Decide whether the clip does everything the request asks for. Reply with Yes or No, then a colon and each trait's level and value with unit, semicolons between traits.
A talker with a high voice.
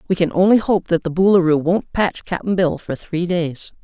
No: medium, 175 Hz